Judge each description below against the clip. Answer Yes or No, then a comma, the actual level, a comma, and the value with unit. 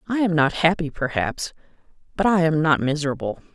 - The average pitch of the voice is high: No, medium, 160 Hz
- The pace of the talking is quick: No, average, 170 wpm